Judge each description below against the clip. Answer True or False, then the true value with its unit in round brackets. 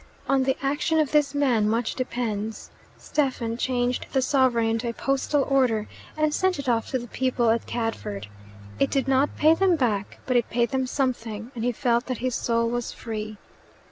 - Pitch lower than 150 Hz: False (245 Hz)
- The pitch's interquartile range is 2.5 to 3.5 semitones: True (3.1 semitones)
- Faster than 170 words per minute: True (190 wpm)